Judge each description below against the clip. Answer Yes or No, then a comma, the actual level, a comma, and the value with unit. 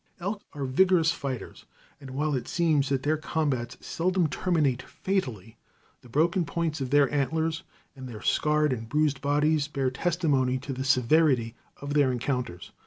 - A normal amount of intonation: Yes, average, 3.6 semitones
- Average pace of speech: Yes, average, 160 wpm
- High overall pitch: No, medium, 145 Hz